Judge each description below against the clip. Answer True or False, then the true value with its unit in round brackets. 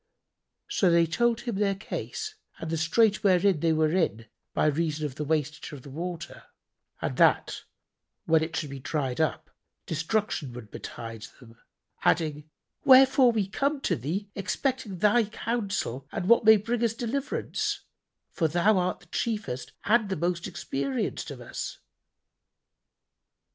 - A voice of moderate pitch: True (175 Hz)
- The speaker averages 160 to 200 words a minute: False (150 wpm)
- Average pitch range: False (6.1 semitones)